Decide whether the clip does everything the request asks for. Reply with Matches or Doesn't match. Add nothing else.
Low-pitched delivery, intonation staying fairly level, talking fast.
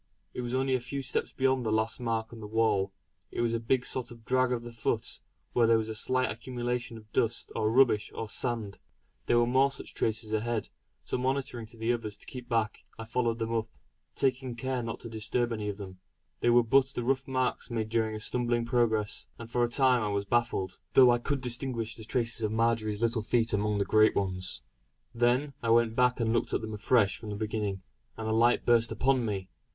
Matches